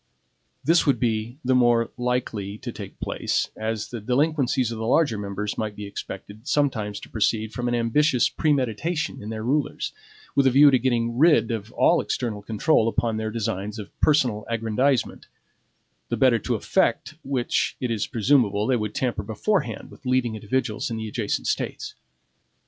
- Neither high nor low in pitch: No, low, 115 Hz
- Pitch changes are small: No, average, 3.3 semitones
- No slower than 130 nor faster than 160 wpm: No, average, 170 wpm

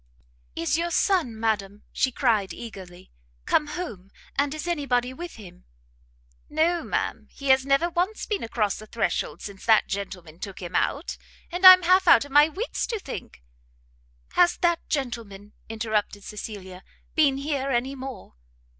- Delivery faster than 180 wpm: No, average, 155 wpm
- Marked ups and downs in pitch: Yes, wide, 7.6 semitones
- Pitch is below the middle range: No, very high, 260 Hz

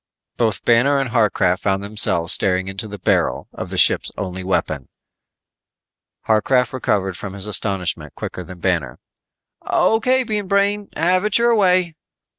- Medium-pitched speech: No, low, 105 Hz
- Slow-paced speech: No, average, 145 wpm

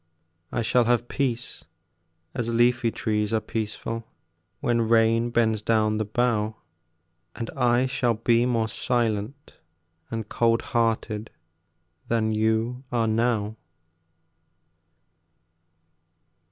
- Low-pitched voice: Yes, low, 115 Hz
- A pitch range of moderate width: No, narrow, 1.5 semitones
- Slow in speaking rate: Yes, slow, 100 wpm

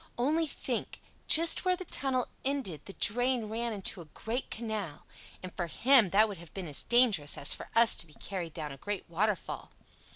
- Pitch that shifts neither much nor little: No, wide, 6.3 semitones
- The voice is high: Yes, high, 215 Hz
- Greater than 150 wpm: Yes, average, 190 wpm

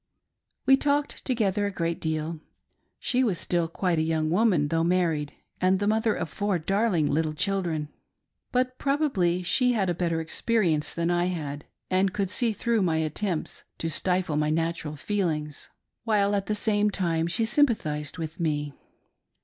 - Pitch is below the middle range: No, medium, 180 Hz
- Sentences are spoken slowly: No, average, 165 wpm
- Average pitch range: Yes, average, 4.6 semitones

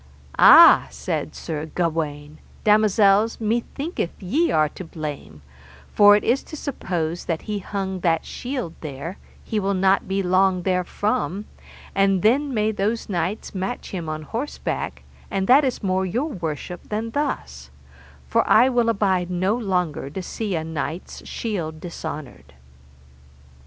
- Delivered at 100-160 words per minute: Yes, average, 140 wpm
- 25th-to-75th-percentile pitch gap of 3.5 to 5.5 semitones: Yes, average, 5.0 semitones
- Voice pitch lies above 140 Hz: Yes, high, 190 Hz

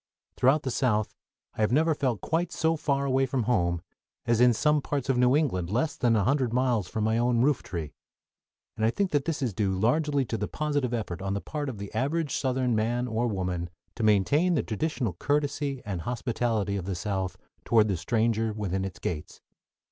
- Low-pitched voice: Yes, low, 120 Hz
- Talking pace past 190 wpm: Yes, average, 200 wpm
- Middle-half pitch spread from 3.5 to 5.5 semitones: Yes, average, 5.1 semitones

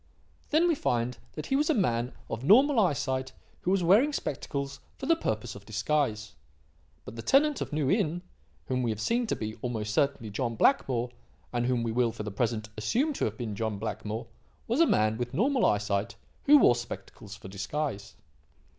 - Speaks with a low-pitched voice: Yes, low, 125 Hz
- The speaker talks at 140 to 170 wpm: No, average, 190 wpm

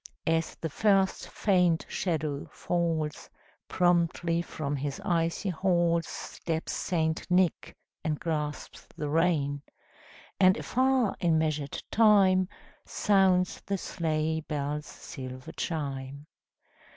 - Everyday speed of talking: No, slow, 105 wpm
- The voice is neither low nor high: Yes, medium, 165 Hz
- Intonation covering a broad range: No, average, 3.2 semitones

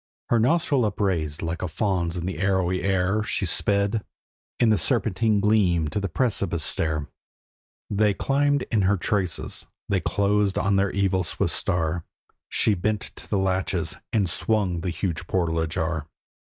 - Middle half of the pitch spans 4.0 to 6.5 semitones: No, average, 3.4 semitones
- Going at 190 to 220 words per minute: No, average, 155 wpm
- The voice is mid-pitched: No, very low, 95 Hz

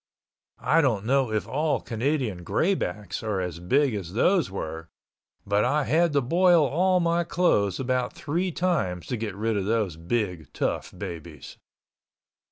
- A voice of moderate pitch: No, low, 120 Hz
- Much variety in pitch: Yes, wide, 8.1 semitones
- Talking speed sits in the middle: Yes, average, 155 wpm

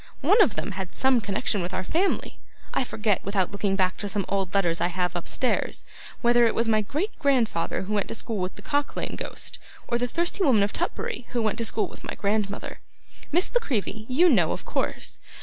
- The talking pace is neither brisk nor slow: No, fast, 220 wpm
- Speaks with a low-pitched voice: No, high, 215 Hz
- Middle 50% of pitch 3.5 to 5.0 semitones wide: Yes, average, 4.5 semitones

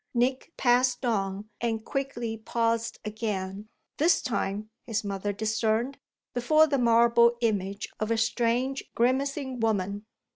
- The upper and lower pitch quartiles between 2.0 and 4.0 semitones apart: Yes, average, 2.7 semitones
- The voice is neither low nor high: No, high, 230 Hz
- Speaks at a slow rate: Yes, slow, 120 wpm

